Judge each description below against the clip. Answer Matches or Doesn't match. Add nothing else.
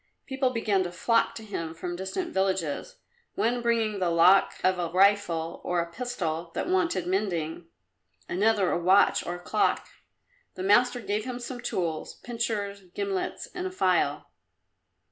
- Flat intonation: Doesn't match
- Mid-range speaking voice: Doesn't match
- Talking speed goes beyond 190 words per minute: Doesn't match